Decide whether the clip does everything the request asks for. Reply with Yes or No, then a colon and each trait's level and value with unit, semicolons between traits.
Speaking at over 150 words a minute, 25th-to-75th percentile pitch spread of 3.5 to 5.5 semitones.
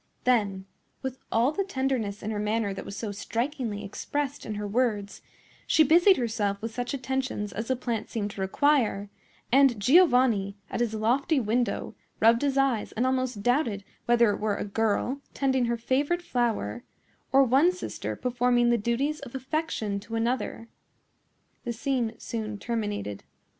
Yes: average, 160 wpm; average, 4.0 semitones